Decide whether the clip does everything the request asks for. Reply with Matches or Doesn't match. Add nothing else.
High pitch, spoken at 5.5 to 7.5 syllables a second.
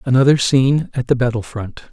Doesn't match